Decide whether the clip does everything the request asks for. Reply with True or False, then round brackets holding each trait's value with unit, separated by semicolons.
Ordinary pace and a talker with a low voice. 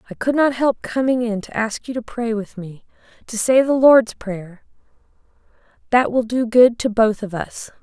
False (190 wpm; 230 Hz)